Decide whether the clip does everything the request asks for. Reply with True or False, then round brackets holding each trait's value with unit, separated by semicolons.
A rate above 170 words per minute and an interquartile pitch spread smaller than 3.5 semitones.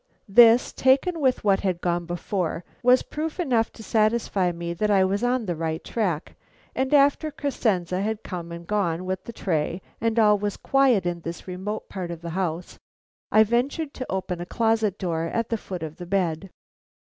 False (190 wpm; 5.0 semitones)